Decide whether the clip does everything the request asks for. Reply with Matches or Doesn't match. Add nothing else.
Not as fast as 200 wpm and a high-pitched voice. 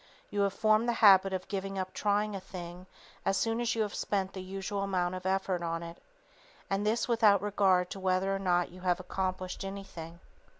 Doesn't match